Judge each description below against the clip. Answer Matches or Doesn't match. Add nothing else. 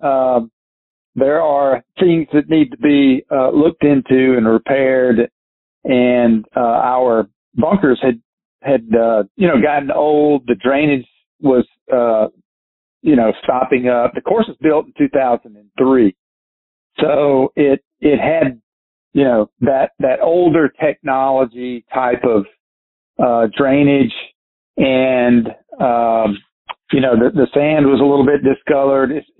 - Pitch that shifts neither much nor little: Matches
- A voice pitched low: Matches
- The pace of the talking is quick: Doesn't match